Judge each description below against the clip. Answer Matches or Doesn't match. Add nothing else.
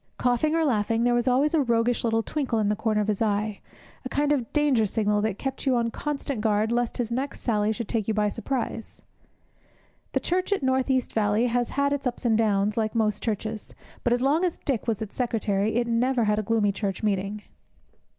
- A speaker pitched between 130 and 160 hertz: Doesn't match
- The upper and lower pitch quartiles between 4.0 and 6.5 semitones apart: Doesn't match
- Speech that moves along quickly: Matches